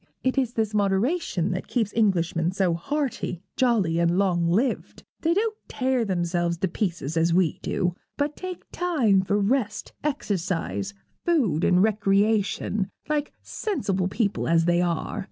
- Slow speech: No, average, 145 wpm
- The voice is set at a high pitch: Yes, high, 195 Hz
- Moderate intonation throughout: No, wide, 6.3 semitones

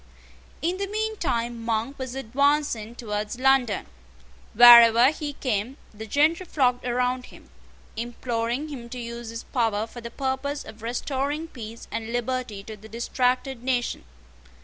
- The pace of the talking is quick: No, average, 145 wpm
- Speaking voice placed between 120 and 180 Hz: No, high, 245 Hz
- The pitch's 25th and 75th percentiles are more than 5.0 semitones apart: No, average, 2.8 semitones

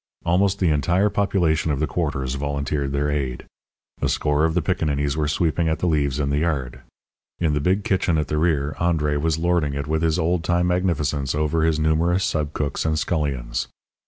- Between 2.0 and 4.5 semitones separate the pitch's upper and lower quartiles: Yes, average, 2.9 semitones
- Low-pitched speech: Yes, very low, 75 Hz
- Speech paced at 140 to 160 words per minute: No, average, 190 wpm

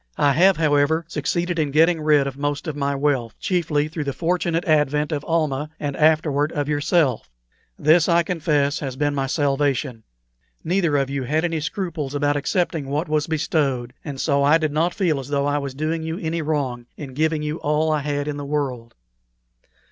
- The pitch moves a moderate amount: No, narrow, 2.2 semitones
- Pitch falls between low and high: Yes, medium, 150 Hz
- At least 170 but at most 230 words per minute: Yes, average, 195 wpm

